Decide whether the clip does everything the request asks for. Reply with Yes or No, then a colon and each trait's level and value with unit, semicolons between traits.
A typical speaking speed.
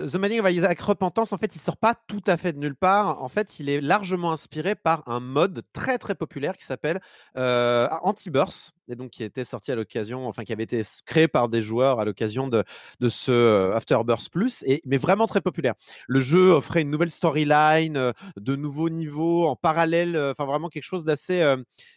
Yes: average, 210 wpm